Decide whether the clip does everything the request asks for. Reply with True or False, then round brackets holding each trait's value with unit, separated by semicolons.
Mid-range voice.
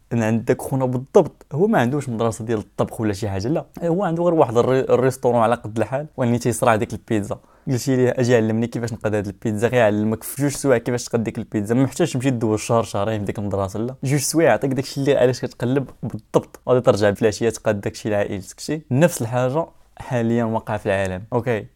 False (120 Hz)